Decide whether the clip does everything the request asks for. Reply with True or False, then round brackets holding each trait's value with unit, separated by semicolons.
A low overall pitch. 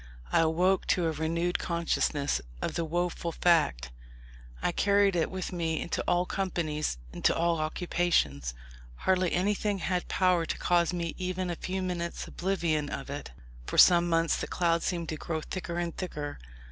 False (170 Hz)